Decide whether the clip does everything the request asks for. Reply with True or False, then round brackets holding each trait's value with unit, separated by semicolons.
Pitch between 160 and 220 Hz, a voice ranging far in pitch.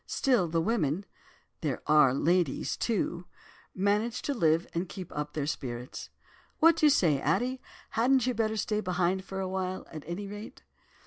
True (185 Hz; 5.7 semitones)